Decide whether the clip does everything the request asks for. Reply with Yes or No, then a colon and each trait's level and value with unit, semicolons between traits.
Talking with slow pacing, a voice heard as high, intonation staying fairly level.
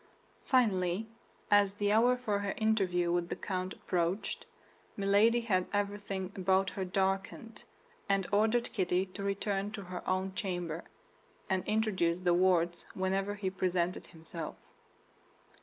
Yes: slow, 130 wpm; high, 195 Hz; narrow, 2.1 semitones